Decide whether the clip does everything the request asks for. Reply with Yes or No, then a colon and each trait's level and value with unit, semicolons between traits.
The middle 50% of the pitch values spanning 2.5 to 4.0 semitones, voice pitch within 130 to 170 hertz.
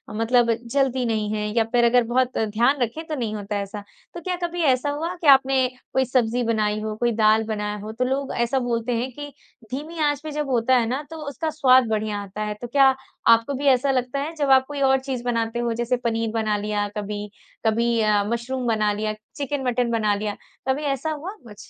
No: average, 3.6 semitones; high, 240 Hz